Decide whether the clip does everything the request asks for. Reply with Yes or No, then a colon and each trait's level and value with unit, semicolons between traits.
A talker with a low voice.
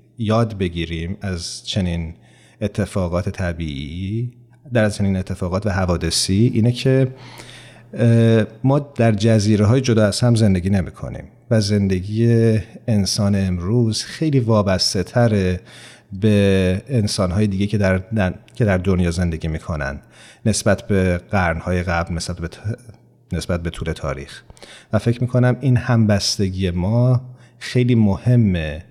Yes: low, 105 Hz